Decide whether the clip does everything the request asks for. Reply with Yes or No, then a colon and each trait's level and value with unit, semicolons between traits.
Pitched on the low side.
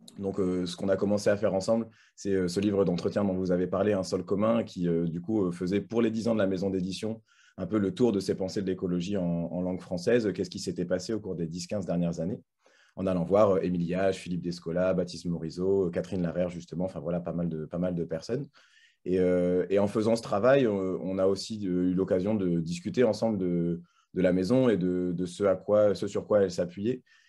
Yes: very low, 95 Hz